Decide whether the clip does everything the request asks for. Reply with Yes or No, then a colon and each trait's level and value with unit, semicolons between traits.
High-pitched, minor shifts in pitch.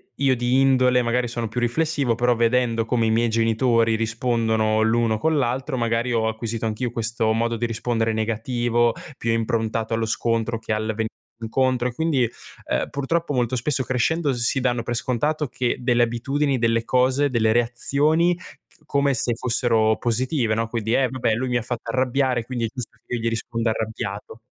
No: low, 120 Hz; narrow, 2.1 semitones